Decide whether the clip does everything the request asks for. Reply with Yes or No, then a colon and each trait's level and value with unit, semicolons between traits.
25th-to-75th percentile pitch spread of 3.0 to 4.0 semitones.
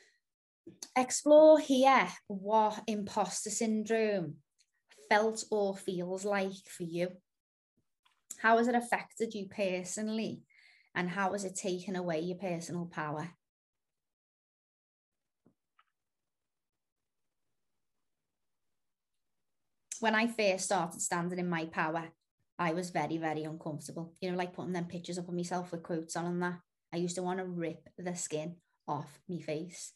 Yes: average, 3.7 semitones